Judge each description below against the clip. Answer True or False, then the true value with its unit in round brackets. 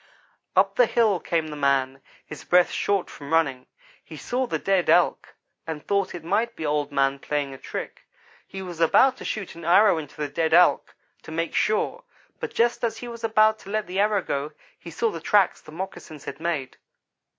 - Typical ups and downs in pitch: False (5.7 semitones)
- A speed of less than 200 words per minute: False (205 wpm)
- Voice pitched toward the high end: False (170 Hz)